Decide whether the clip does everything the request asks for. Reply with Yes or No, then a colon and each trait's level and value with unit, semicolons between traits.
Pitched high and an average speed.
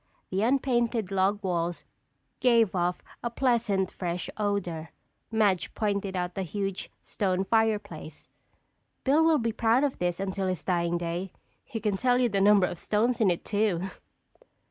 Yes: high, 200 Hz; average, 155 wpm